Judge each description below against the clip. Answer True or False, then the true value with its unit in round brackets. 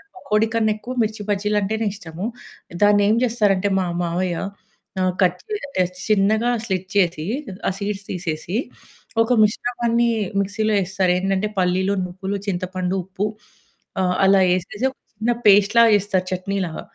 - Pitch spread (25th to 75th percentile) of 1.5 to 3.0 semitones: True (2.5 semitones)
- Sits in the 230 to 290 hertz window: False (200 Hz)